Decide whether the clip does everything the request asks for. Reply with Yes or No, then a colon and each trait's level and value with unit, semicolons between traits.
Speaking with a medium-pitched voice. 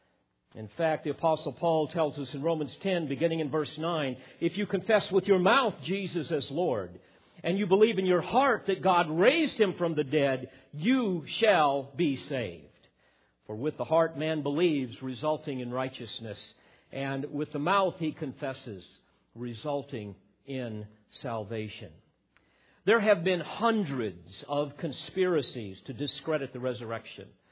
Yes: medium, 150 Hz